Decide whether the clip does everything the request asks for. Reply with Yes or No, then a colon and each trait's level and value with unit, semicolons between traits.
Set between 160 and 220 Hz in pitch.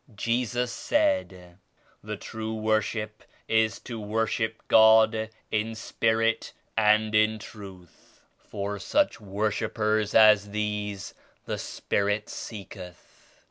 No: low, 110 Hz